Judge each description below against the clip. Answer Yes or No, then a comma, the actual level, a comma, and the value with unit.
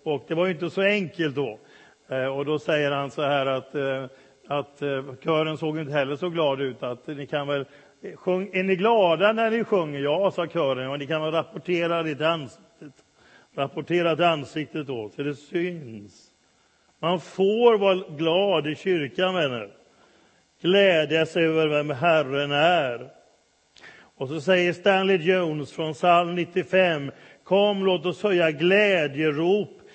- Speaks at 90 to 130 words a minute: No, average, 145 wpm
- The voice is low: No, medium, 160 Hz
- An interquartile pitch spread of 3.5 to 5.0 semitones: Yes, average, 4.3 semitones